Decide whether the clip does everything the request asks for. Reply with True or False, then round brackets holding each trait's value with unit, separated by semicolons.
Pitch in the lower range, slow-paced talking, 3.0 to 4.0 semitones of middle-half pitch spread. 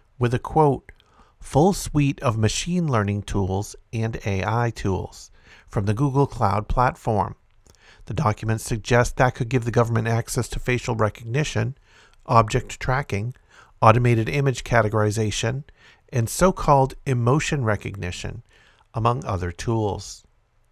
True (115 Hz; 120 wpm; 3.4 semitones)